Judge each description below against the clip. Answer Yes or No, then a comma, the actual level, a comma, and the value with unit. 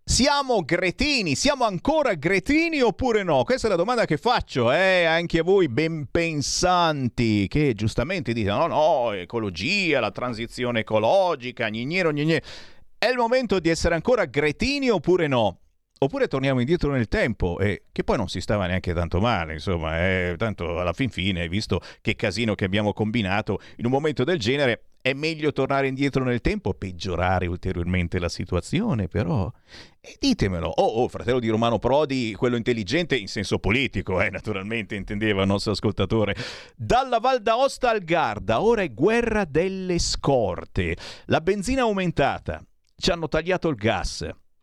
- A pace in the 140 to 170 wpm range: Yes, average, 160 wpm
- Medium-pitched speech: No, low, 125 Hz